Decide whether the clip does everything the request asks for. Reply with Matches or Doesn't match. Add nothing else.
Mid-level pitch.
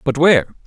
Matches